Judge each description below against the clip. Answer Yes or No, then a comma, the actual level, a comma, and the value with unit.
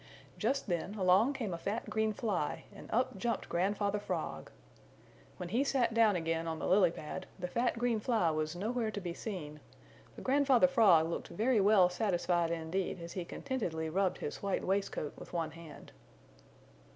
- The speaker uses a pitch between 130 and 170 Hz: No, high, 195 Hz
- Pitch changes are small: No, average, 5.0 semitones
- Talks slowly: No, average, 175 wpm